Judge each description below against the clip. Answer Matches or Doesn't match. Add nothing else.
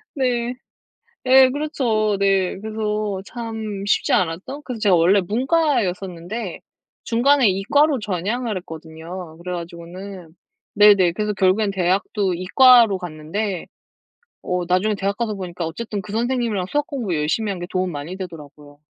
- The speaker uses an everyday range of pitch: Matches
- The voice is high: Matches